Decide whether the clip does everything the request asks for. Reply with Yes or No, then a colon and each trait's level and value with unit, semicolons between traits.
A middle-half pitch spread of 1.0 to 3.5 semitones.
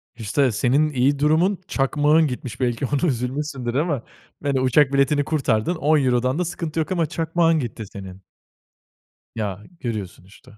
No: average, 4.3 semitones